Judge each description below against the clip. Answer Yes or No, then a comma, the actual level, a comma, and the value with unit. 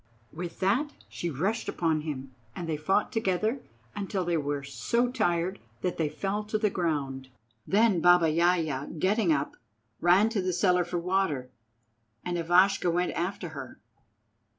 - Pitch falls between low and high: Yes, medium, 175 Hz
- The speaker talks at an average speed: Yes, average, 155 wpm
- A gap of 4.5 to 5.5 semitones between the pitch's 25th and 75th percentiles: No, average, 3.8 semitones